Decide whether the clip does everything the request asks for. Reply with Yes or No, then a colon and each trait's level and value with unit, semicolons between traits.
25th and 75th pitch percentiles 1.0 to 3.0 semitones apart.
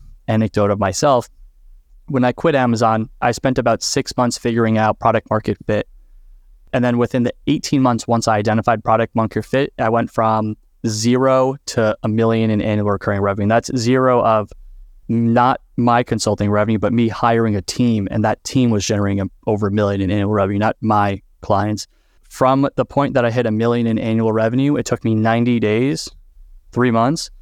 Yes: narrow, 2.5 semitones